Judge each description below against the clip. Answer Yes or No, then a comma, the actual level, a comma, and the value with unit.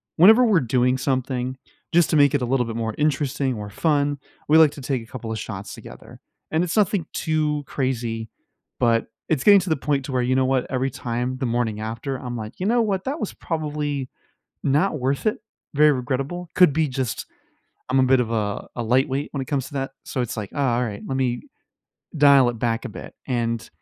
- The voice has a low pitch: Yes, low, 130 Hz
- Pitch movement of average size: Yes, average, 3.6 semitones